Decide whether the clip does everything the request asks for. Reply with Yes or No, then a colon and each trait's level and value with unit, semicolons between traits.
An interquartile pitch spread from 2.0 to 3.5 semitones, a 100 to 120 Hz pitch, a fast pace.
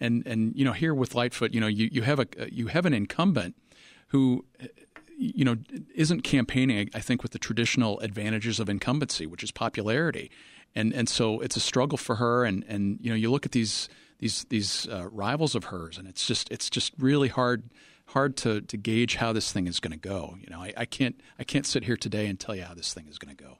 Yes: average, 3.2 semitones; low, 115 Hz; fast, 235 wpm